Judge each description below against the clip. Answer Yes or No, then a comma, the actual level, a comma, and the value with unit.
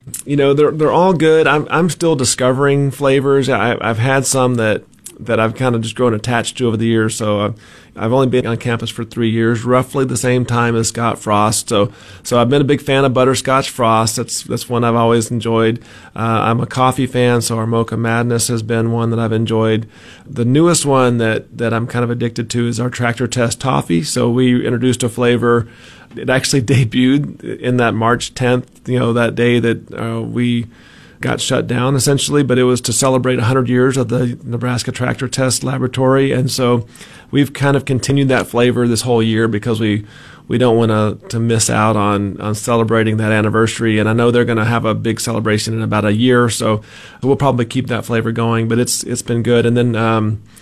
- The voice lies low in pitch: Yes, low, 120 Hz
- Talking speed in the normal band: No, fast, 215 wpm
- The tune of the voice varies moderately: No, narrow, 2.1 semitones